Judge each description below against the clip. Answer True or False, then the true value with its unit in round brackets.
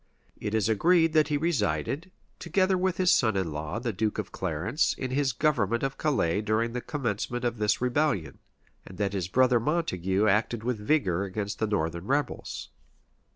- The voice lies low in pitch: True (110 Hz)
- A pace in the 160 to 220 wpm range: True (175 wpm)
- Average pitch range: False (6.5 semitones)